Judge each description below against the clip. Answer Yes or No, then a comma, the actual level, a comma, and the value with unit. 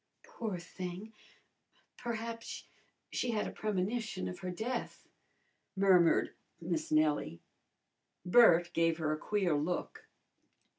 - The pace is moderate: No, slow, 105 wpm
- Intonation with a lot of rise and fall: No, average, 4.9 semitones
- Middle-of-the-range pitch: Yes, medium, 180 Hz